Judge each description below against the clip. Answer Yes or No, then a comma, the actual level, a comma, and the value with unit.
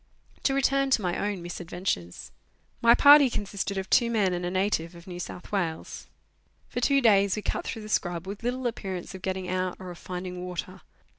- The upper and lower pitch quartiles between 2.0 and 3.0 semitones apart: No, average, 3.9 semitones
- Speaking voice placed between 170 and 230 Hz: Yes, high, 190 Hz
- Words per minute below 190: No, average, 200 wpm